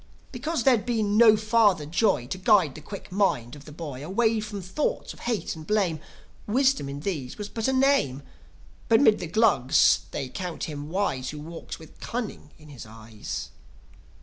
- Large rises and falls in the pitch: Yes, wide, 7.3 semitones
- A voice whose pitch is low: No, medium, 185 Hz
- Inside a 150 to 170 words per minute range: No, average, 180 wpm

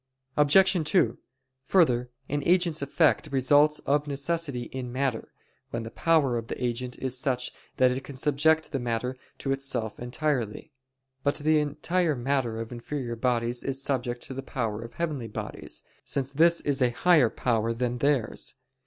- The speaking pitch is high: No, low, 135 Hz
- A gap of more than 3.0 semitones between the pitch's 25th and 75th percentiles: Yes, average, 3.5 semitones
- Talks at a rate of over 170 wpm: No, average, 160 wpm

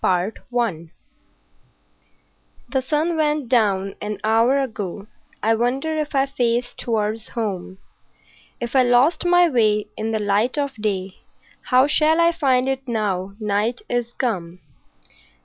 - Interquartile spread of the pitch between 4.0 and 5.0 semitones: Yes, average, 4.4 semitones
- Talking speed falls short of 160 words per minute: Yes, slow, 135 wpm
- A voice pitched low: No, high, 235 Hz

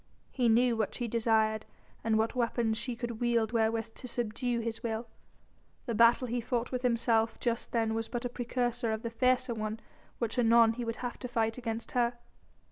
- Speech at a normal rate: Yes, average, 195 wpm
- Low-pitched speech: No, high, 230 Hz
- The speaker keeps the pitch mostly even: Yes, narrow, 1.4 semitones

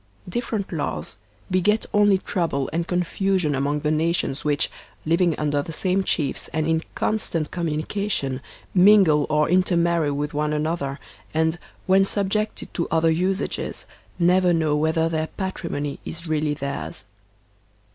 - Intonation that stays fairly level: No, average, 3.6 semitones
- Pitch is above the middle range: No, medium, 165 Hz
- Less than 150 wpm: Yes, slow, 135 wpm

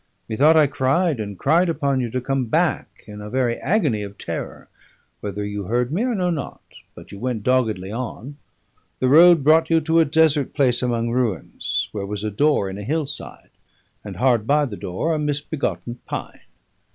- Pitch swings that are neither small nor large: No, wide, 5.9 semitones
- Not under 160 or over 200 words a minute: Yes, average, 190 wpm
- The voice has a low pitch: Yes, low, 130 Hz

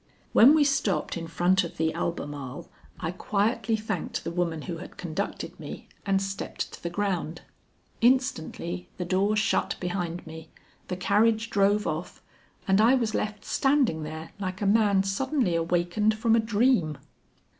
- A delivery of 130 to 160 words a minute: Yes, average, 155 wpm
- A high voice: Yes, high, 195 Hz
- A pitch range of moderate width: Yes, average, 4.2 semitones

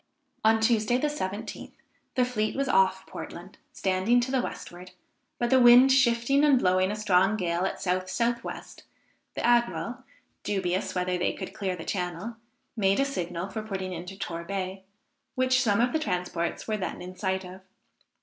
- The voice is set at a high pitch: Yes, high, 205 Hz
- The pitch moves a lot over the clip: No, average, 4.7 semitones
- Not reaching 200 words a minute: Yes, average, 170 wpm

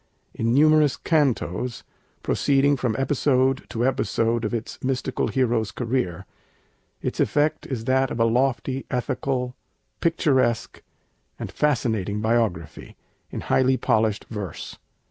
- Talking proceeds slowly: Yes, slow, 115 wpm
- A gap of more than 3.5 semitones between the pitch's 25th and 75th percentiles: No, average, 2.9 semitones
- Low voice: Yes, low, 125 Hz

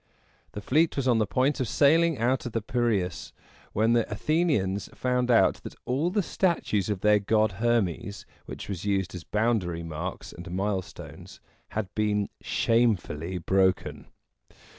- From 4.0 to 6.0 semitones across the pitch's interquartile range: Yes, average, 4.7 semitones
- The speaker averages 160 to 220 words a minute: No, average, 150 wpm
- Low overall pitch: Yes, low, 110 Hz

